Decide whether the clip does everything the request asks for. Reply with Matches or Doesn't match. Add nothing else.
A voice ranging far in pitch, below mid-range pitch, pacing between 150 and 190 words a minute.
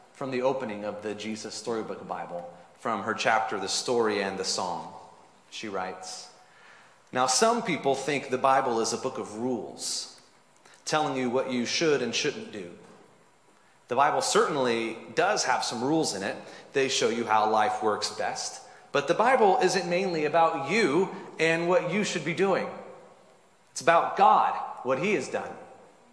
Matches